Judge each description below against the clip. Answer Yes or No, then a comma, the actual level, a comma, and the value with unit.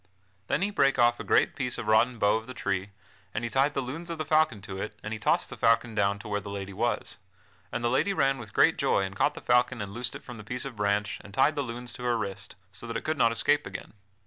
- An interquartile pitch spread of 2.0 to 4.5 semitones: Yes, average, 4.1 semitones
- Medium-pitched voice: No, low, 115 Hz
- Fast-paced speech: Yes, fast, 280 wpm